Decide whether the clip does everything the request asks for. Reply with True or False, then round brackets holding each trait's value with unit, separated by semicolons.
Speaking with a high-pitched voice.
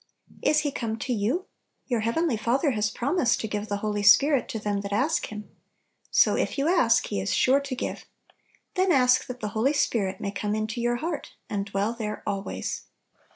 True (230 Hz)